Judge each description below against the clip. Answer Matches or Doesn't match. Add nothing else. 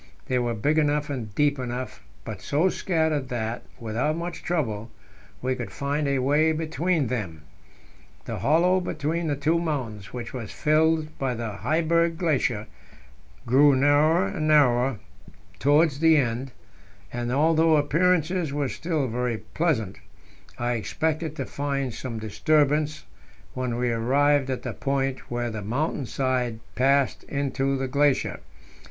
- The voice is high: Doesn't match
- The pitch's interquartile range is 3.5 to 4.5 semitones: Matches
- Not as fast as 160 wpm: Matches